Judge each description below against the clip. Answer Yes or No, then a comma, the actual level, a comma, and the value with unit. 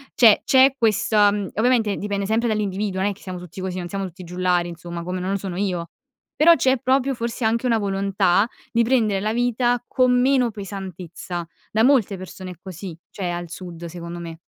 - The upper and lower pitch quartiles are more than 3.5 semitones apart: Yes, average, 4.3 semitones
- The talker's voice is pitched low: No, high, 200 Hz